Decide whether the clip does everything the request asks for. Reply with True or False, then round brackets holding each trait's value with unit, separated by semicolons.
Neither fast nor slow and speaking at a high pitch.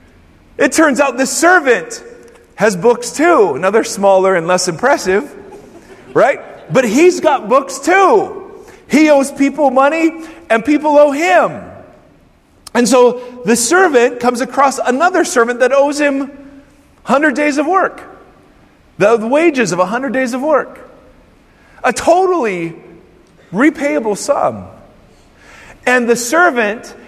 False (125 wpm; 275 Hz)